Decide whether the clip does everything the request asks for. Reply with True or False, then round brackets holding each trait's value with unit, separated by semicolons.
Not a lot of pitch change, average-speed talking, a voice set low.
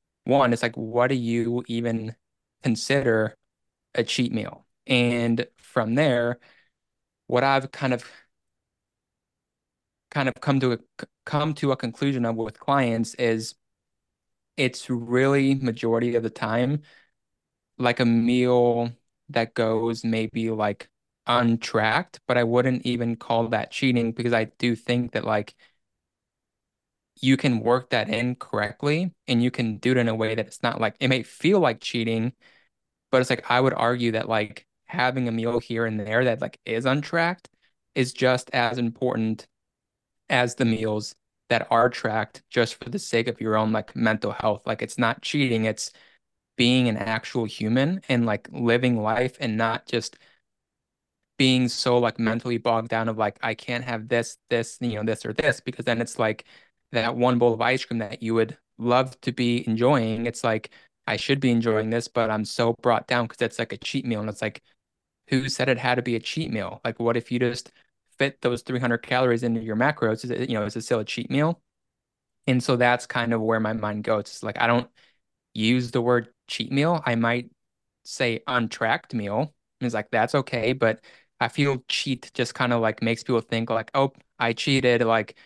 True (1.8 semitones; 185 wpm; 120 Hz)